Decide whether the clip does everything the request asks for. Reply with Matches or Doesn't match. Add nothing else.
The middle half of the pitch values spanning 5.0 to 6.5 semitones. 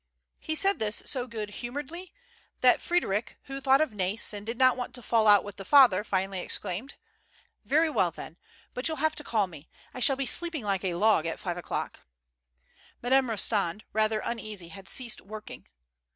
Matches